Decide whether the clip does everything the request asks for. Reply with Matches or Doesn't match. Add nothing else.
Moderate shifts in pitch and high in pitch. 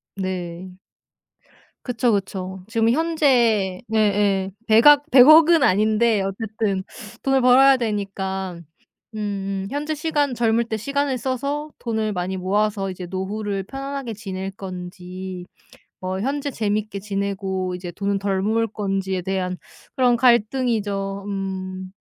Matches